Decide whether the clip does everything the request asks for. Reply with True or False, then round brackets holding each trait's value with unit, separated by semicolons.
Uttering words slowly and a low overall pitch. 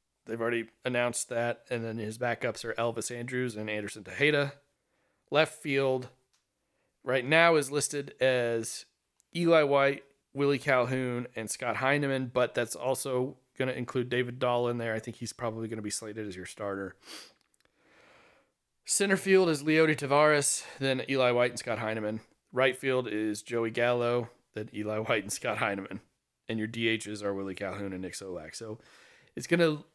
False (170 wpm; 120 Hz)